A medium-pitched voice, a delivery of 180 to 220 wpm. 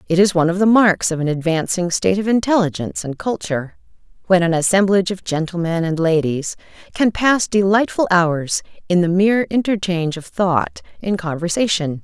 No: medium, 180 Hz; average, 165 wpm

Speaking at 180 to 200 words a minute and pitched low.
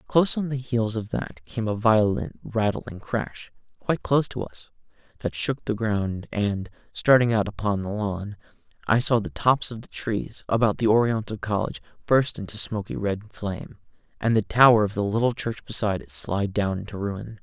Yes: average, 185 wpm; low, 110 Hz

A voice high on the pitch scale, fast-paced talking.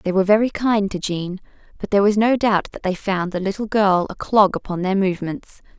Yes: high, 195 Hz; fast, 230 wpm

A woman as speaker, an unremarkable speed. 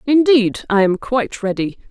Yes: female; average, 155 wpm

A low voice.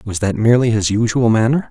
Yes: low, 110 Hz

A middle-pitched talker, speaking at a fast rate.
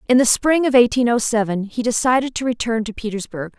No: high, 235 Hz; fast, 215 wpm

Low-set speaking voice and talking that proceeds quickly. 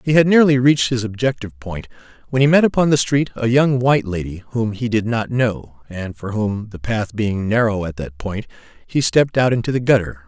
Yes: low, 115 Hz; fast, 220 wpm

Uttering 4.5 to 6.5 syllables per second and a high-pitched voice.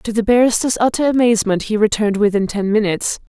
No: 6.7 syllables/s; high, 220 Hz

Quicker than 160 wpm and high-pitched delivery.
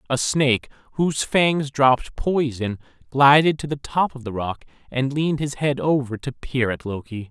No: average, 180 wpm; low, 135 Hz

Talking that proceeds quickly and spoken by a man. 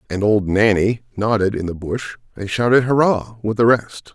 No: average, 190 wpm; male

